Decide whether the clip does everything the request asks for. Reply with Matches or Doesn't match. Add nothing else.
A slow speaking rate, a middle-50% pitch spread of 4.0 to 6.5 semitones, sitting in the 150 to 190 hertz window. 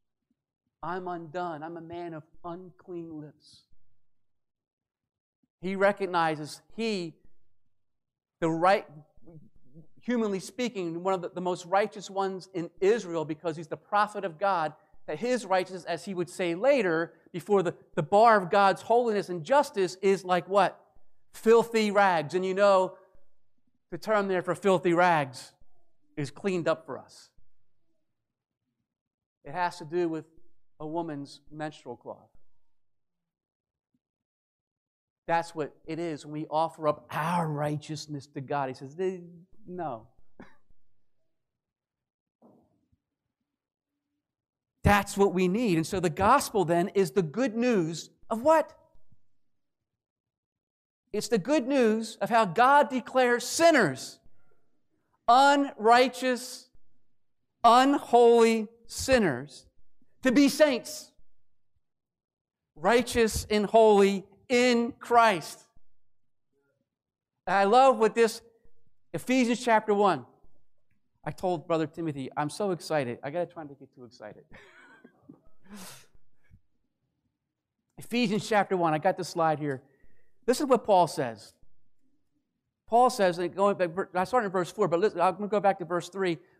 Matches